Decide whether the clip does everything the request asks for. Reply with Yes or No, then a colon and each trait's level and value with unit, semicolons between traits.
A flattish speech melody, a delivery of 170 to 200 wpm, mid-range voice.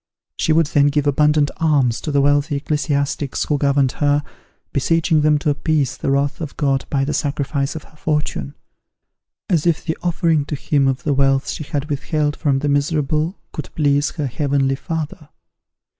Yes: narrow, 1.7 semitones; average, 175 wpm; medium, 145 Hz